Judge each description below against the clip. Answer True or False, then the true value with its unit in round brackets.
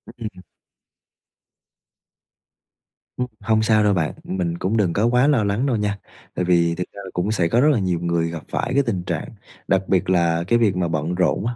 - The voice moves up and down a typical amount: True (4.4 semitones)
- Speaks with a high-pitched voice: False (95 Hz)